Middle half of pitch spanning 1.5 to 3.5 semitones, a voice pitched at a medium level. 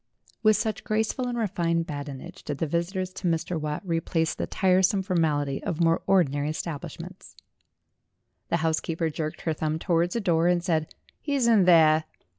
Yes: average, 3.1 semitones; medium, 170 Hz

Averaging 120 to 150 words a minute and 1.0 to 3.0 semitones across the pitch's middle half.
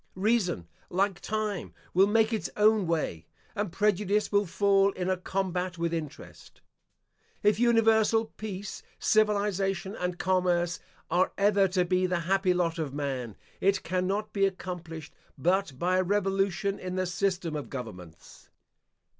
Yes: average, 140 wpm; average, 2.7 semitones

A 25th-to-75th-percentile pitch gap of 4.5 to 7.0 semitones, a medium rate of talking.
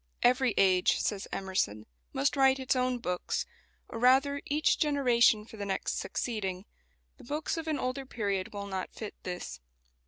Yes: wide, 5.6 semitones; average, 160 wpm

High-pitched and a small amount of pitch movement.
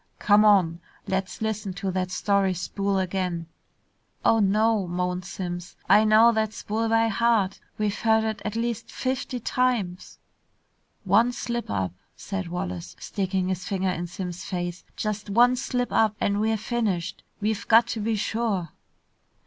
No: high, 205 Hz; average, 3.4 semitones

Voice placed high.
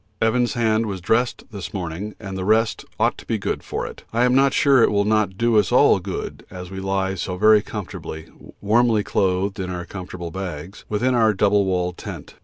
No: low, 100 Hz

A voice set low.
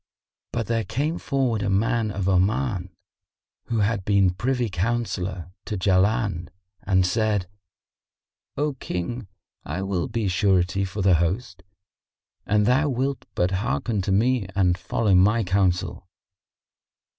Yes: low, 100 Hz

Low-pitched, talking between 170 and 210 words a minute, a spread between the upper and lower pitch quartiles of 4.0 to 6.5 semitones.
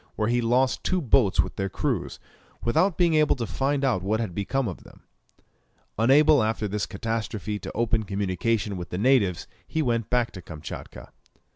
Yes: low, 115 Hz; average, 175 wpm; average, 4.7 semitones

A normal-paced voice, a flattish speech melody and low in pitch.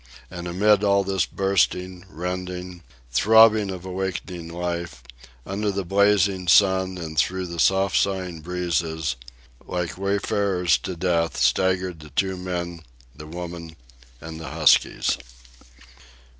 No: slow, 120 wpm; narrow, 2.1 semitones; very low, 90 Hz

